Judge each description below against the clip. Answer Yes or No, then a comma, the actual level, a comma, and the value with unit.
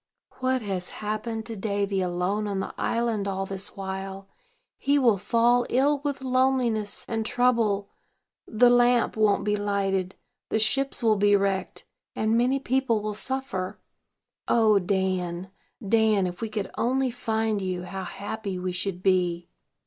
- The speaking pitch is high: Yes, high, 210 Hz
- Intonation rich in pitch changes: No, average, 3.6 semitones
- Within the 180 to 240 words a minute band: No, average, 150 wpm